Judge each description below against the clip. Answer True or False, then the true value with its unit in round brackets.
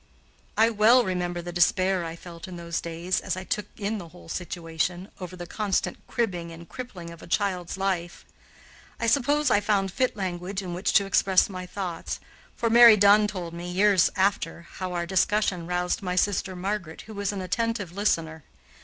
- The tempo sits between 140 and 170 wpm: False (185 wpm)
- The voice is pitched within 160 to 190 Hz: True (185 Hz)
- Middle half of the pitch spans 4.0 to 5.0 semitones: False (2.9 semitones)